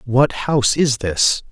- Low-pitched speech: Yes, low, 125 Hz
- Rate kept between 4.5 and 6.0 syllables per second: No, 3.7 syllables/s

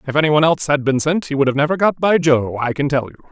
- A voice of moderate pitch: Yes, medium, 145 Hz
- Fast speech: Yes, fast, 310 wpm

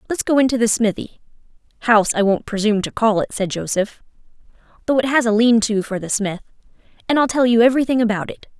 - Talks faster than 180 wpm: Yes, average, 195 wpm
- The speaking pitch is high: Yes, high, 225 Hz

